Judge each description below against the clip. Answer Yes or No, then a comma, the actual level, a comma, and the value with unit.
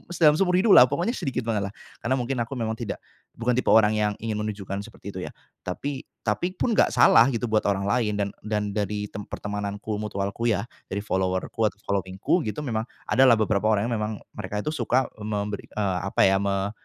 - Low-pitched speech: Yes, low, 105 Hz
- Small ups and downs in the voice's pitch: No, average, 3.3 semitones